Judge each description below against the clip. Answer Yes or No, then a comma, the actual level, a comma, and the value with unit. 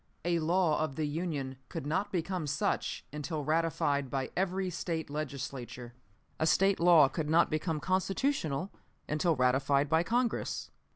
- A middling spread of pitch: Yes, average, 3.8 semitones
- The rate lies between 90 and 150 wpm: Yes, average, 140 wpm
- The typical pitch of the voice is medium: Yes, medium, 155 Hz